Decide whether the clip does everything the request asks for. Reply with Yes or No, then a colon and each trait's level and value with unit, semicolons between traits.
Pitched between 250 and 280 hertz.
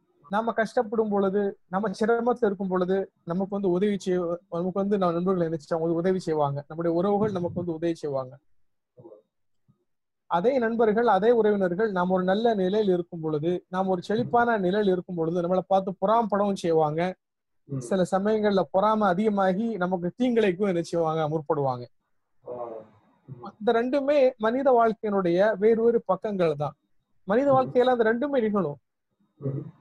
No: high, 190 Hz